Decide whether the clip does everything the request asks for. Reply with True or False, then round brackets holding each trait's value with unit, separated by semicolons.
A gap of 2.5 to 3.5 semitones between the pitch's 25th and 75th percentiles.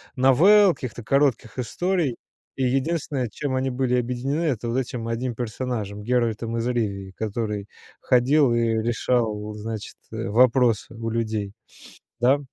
True (2.8 semitones)